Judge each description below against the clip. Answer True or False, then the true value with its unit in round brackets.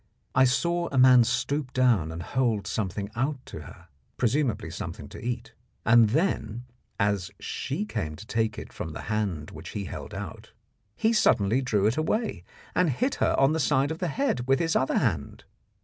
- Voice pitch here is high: False (120 Hz)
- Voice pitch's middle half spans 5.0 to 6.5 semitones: True (5.3 semitones)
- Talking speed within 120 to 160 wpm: False (185 wpm)